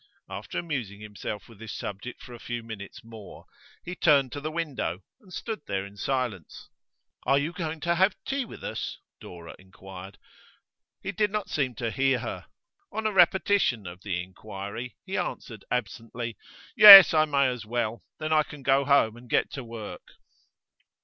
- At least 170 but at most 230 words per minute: Yes, average, 175 wpm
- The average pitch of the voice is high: No, low, 125 Hz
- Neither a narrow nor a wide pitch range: No, wide, 6.7 semitones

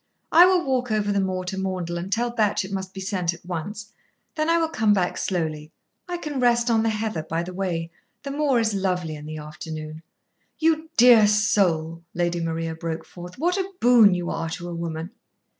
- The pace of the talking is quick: Yes, fast, 210 wpm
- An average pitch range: No, wide, 5.8 semitones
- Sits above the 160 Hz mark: Yes, high, 190 Hz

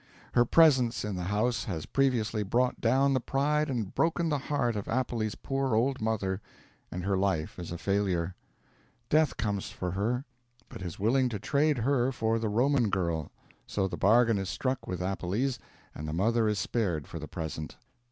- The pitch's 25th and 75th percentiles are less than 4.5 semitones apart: No, average, 5.2 semitones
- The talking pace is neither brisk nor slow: Yes, average, 180 wpm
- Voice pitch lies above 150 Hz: No, low, 110 Hz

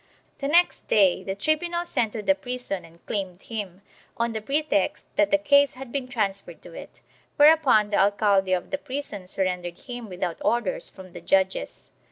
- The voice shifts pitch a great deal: Yes, wide, 6.7 semitones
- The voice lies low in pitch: No, high, 215 Hz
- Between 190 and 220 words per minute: No, average, 180 wpm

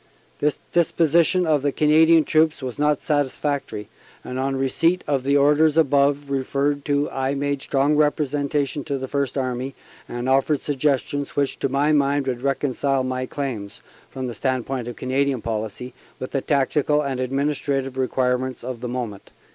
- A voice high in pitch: No, medium, 140 Hz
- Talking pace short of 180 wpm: Yes, average, 155 wpm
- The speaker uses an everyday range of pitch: No, narrow, 2.1 semitones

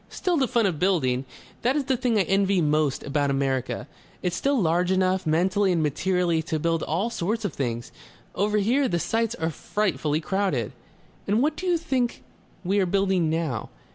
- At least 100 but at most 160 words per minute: No, average, 185 wpm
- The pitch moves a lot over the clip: Yes, wide, 5.8 semitones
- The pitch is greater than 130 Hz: Yes, medium, 185 Hz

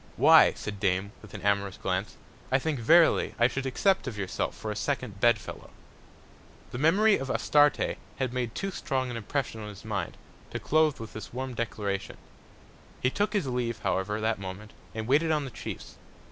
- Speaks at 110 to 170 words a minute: No, average, 190 wpm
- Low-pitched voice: Yes, low, 120 Hz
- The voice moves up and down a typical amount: Yes, average, 4.9 semitones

